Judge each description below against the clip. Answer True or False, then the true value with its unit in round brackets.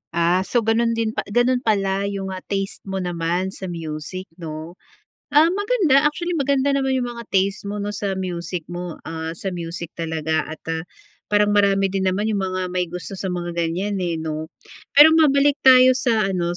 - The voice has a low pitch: False (195 Hz)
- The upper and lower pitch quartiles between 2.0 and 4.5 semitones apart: False (5.0 semitones)